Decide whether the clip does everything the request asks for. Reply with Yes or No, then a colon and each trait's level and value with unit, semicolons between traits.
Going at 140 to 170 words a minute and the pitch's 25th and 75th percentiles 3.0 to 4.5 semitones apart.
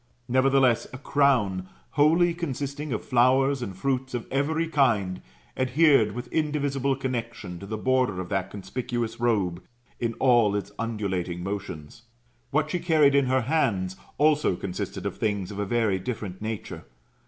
No: average, 150 wpm; wide, 5.5 semitones